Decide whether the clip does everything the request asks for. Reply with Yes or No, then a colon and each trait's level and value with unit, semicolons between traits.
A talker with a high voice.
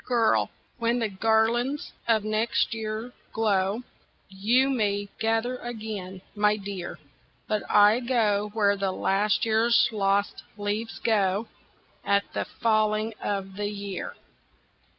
Yes: high, 215 Hz